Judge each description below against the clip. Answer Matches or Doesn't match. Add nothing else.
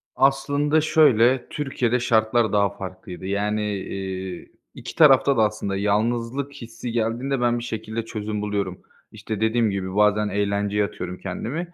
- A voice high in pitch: Doesn't match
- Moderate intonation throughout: Matches